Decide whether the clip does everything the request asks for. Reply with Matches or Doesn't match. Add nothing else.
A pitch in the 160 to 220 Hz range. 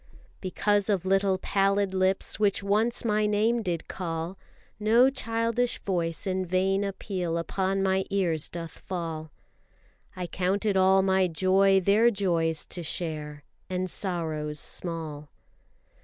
Matches